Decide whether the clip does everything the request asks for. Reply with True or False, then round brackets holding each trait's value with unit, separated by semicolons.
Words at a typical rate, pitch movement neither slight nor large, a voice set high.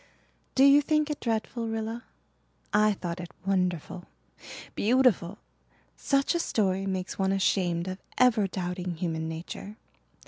False (130 wpm; 4.4 semitones; 195 Hz)